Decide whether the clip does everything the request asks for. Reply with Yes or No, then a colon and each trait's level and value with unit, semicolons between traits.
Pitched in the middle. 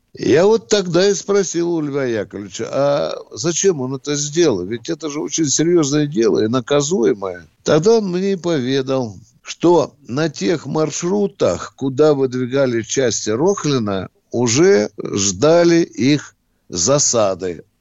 Yes: medium, 145 Hz